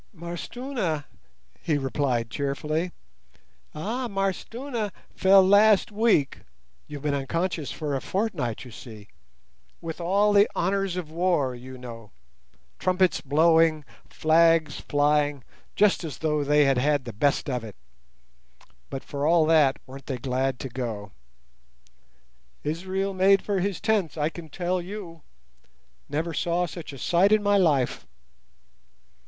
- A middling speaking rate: No, slow, 125 wpm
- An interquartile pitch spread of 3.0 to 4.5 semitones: No, wide, 5.6 semitones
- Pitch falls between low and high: Yes, medium, 155 Hz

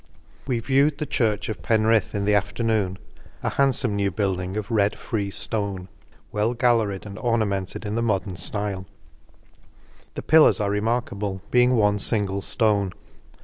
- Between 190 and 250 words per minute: No, average, 155 wpm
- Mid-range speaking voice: No, low, 105 Hz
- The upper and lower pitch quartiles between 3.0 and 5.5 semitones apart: No, narrow, 2.6 semitones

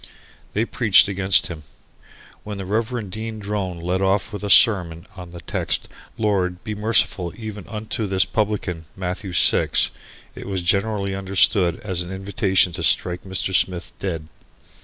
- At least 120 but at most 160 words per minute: Yes, average, 155 wpm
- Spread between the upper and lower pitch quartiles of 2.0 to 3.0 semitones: Yes, average, 2.7 semitones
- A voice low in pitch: Yes, very low, 95 Hz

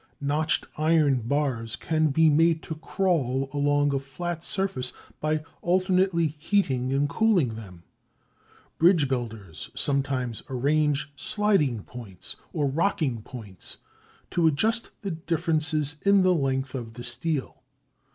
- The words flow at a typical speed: No, slow, 120 wpm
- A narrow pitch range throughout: No, average, 4.3 semitones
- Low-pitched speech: No, medium, 145 Hz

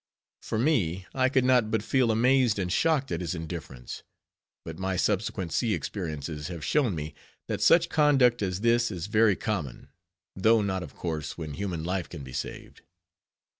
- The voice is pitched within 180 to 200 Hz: No, low, 100 Hz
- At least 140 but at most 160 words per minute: No, average, 170 wpm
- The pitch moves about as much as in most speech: No, wide, 6.3 semitones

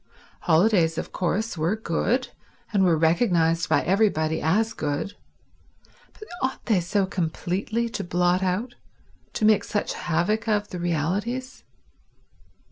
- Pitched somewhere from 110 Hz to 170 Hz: No, medium, 185 Hz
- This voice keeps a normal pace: No, slow, 125 wpm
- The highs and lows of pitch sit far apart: No, average, 4.6 semitones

